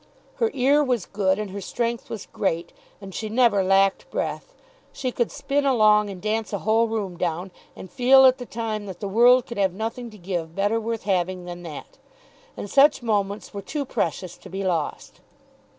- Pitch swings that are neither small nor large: Yes, average, 3.9 semitones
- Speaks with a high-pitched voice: Yes, high, 210 Hz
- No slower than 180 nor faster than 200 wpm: Yes, average, 195 wpm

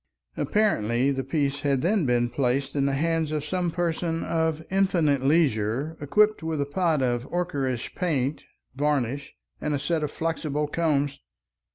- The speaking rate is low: No, average, 155 wpm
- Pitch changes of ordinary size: Yes, average, 3.3 semitones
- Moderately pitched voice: Yes, medium, 150 Hz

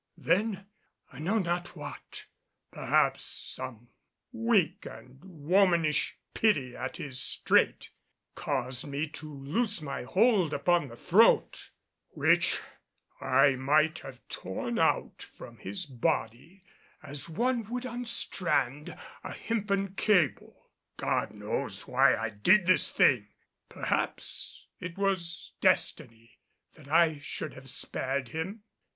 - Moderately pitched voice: Yes, medium, 160 Hz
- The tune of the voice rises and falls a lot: Yes, wide, 6.4 semitones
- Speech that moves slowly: Yes, slow, 115 wpm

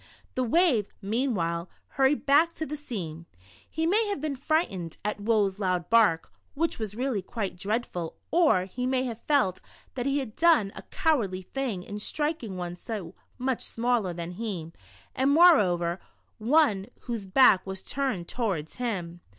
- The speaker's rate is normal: Yes, average, 160 wpm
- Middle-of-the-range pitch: No, high, 225 Hz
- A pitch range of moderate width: No, wide, 6.8 semitones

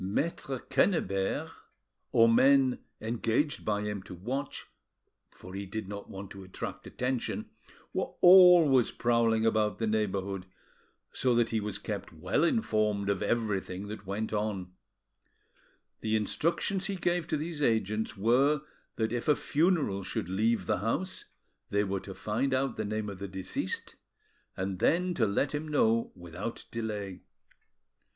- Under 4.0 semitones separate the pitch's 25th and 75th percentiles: No, average, 5.3 semitones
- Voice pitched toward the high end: No, low, 110 Hz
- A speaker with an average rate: Yes, average, 145 wpm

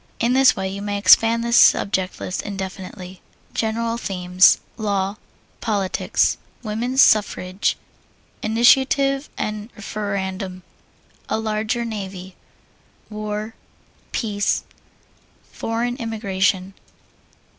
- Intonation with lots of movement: No, average, 3.1 semitones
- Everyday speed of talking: No, slow, 90 wpm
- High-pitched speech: Yes, high, 210 Hz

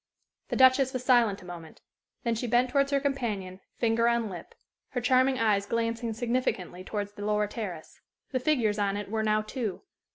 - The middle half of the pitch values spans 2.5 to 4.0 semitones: Yes, average, 3.6 semitones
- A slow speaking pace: No, average, 185 wpm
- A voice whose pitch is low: No, high, 225 Hz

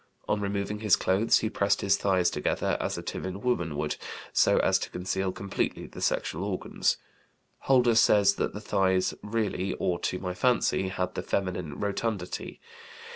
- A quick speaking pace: No, average, 165 wpm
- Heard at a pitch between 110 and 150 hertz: No, low, 100 Hz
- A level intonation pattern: Yes, narrow, 2.2 semitones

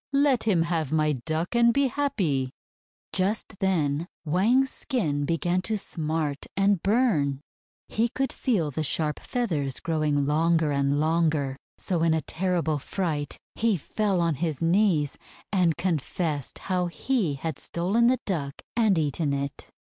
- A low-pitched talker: No, medium, 165 Hz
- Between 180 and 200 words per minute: No, average, 145 wpm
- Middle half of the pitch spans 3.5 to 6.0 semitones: Yes, average, 4.8 semitones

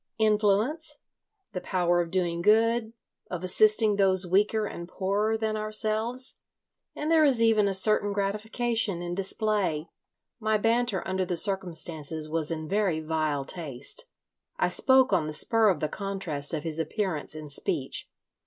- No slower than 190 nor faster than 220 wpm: No, average, 155 wpm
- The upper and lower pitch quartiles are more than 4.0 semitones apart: Yes, average, 4.4 semitones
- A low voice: No, high, 195 Hz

